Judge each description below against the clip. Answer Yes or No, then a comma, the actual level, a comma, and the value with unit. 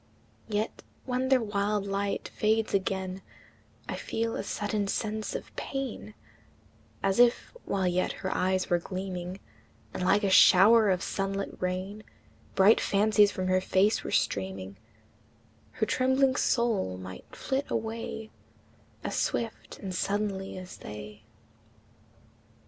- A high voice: Yes, high, 200 Hz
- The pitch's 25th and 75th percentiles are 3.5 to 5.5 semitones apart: No, average, 2.9 semitones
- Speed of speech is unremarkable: No, slow, 130 wpm